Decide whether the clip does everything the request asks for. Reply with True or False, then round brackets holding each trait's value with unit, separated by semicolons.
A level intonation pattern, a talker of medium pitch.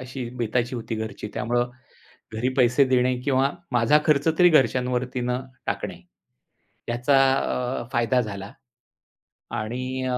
False (1.6 semitones; 125 Hz)